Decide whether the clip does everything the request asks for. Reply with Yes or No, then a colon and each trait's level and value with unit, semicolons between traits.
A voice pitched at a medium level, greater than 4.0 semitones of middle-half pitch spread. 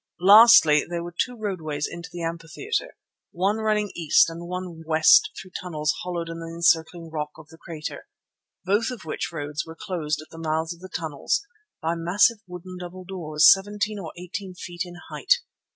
No: medium, 170 Hz; average, 2.9 semitones